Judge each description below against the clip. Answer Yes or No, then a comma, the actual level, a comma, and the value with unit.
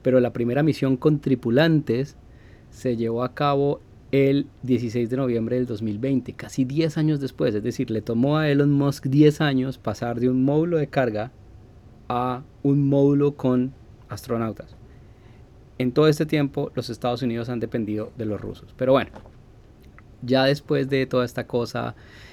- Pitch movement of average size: Yes, average, 3.2 semitones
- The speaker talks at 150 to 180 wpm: Yes, average, 160 wpm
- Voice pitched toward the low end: Yes, low, 125 Hz